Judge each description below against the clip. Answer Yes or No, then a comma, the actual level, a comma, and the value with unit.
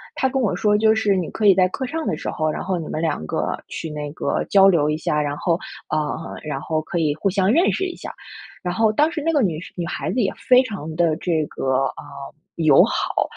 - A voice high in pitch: No, medium, 180 Hz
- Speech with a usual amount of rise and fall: No, wide, 5.9 semitones